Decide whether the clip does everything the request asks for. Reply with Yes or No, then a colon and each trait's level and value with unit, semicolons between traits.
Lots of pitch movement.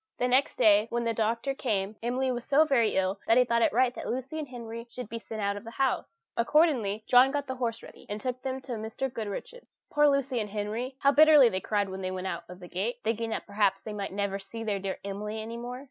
No: average, 3.7 semitones